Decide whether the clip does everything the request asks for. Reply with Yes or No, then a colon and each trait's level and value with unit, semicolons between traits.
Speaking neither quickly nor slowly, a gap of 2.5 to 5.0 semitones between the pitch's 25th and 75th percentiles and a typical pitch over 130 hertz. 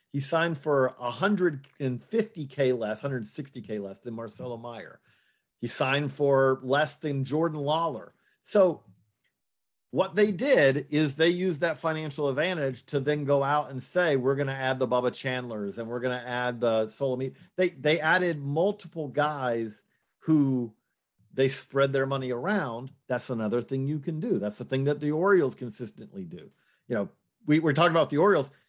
Yes: average, 165 wpm; average, 3.9 semitones; medium, 140 Hz